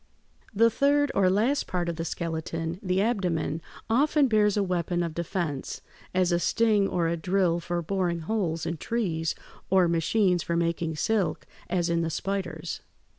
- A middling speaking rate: Yes, average, 170 wpm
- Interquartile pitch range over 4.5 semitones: No, average, 3.5 semitones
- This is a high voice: No, medium, 180 Hz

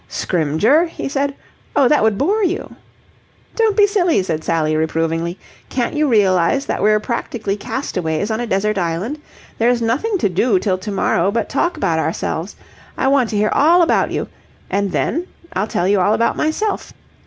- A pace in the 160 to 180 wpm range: Yes, average, 175 wpm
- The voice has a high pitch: Yes, high, 215 Hz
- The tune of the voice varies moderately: No, wide, 7.5 semitones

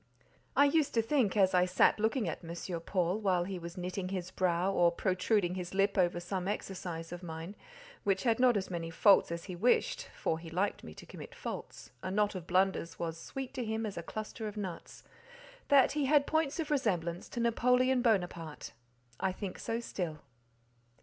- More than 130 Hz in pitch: Yes, high, 190 Hz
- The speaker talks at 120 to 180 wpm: No, average, 195 wpm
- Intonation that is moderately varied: Yes, average, 4.3 semitones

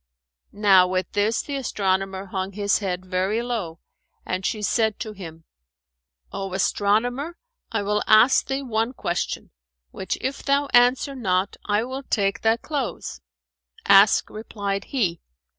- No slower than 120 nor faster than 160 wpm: Yes, average, 140 wpm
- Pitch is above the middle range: Yes, high, 205 Hz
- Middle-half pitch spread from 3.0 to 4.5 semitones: Yes, average, 4.1 semitones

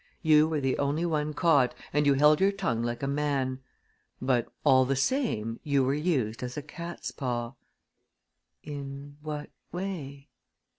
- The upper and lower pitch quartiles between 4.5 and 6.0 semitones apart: No, average, 2.8 semitones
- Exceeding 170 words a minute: No, average, 155 wpm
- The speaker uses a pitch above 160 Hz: No, medium, 140 Hz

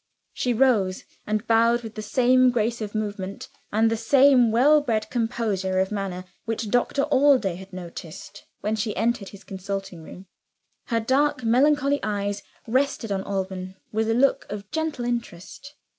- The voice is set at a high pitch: Yes, high, 225 Hz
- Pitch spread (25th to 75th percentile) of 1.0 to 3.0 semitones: No, average, 4.0 semitones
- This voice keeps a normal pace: Yes, average, 160 wpm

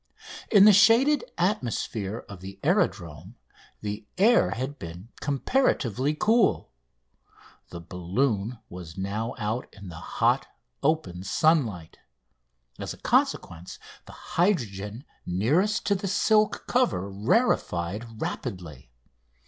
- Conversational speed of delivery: No, slow, 110 wpm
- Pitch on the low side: Yes, low, 115 Hz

